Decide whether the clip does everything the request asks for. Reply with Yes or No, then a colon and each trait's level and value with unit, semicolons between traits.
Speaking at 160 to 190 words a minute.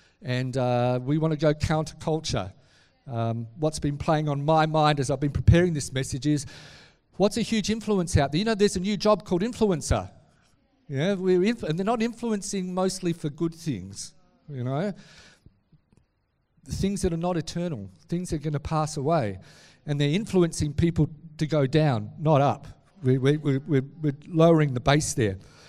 Yes: average, 180 wpm